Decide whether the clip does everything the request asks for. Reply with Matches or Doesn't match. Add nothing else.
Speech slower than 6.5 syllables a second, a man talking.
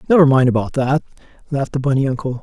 Doesn't match